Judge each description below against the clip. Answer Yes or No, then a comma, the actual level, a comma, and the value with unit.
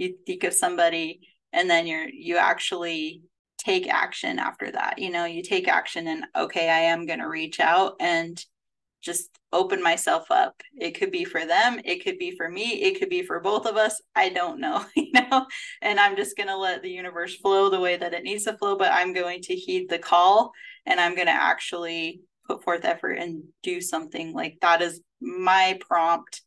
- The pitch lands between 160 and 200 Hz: Yes, high, 190 Hz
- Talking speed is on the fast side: Yes, fast, 210 wpm